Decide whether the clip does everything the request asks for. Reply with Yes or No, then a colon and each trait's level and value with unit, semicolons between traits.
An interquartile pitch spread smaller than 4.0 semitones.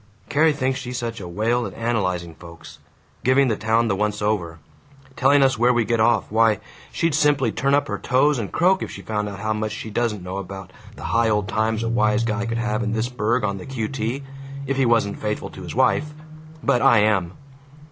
Yes: average, 3.1 semitones